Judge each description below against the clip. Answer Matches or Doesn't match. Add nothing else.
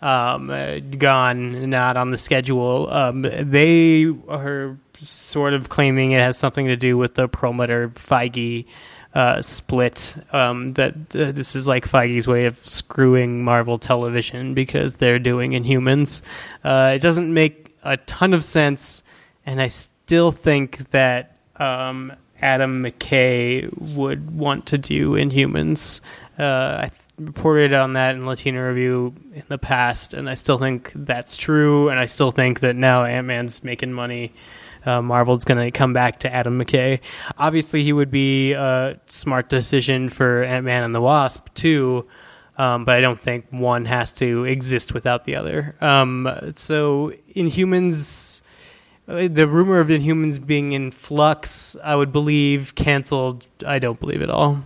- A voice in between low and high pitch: Doesn't match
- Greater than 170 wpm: Doesn't match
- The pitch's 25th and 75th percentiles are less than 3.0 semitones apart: Matches